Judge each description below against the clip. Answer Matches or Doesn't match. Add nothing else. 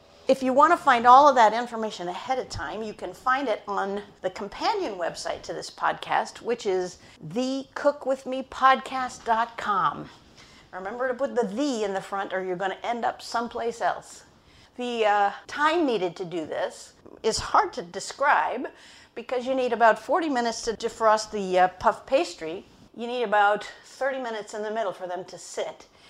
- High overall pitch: Matches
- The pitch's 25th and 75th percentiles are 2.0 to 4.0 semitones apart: Doesn't match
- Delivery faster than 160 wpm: Matches